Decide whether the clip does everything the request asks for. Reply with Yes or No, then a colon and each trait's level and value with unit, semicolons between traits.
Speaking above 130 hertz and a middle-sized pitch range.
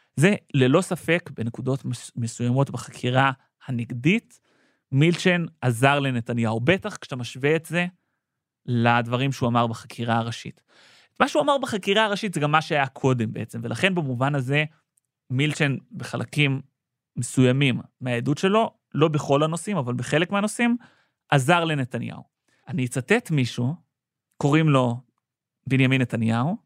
Yes: medium, 140 Hz; average, 4.9 semitones